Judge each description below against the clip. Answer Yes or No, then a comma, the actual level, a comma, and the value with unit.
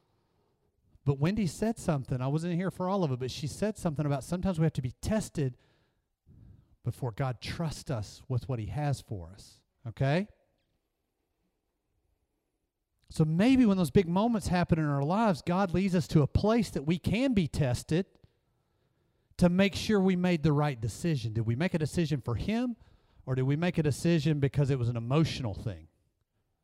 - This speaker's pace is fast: No, average, 180 wpm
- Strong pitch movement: Yes, wide, 6.1 semitones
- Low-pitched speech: No, medium, 155 Hz